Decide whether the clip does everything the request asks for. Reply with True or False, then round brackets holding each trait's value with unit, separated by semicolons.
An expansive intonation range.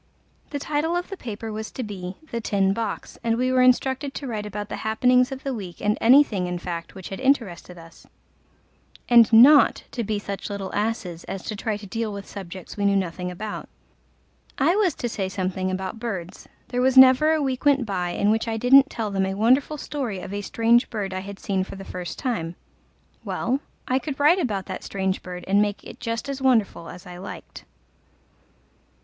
False (4.9 semitones)